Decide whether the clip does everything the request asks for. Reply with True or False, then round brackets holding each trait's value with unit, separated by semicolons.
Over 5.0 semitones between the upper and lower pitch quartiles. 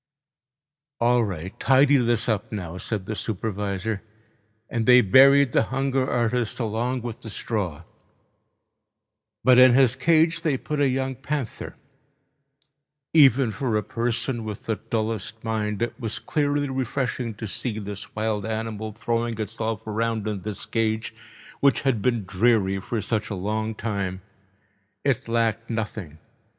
False (3.1 semitones)